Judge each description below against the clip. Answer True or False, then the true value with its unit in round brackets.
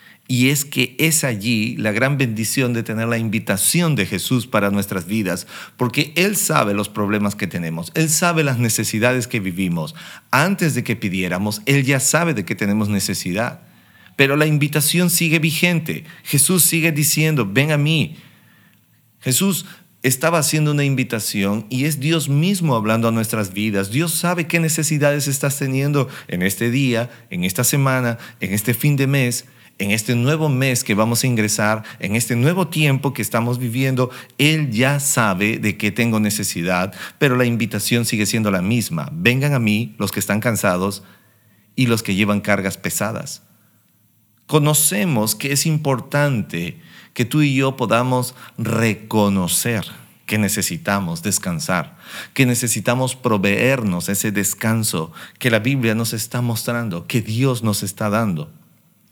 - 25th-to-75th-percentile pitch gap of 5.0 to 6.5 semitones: True (5.3 semitones)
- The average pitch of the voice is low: True (120 Hz)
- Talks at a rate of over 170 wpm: False (155 wpm)